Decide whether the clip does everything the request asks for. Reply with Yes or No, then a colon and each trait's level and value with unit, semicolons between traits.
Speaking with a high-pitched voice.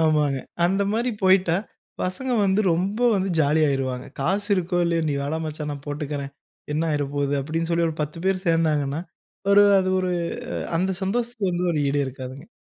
No: medium, 165 Hz